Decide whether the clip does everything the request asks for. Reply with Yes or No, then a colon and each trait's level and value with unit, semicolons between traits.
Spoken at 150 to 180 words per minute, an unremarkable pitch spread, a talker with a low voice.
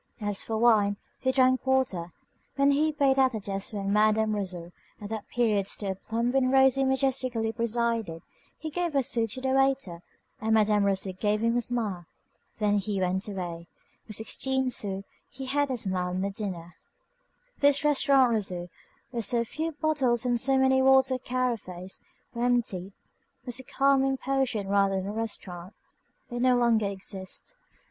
No: average, 170 wpm; average, 4.9 semitones; high, 230 Hz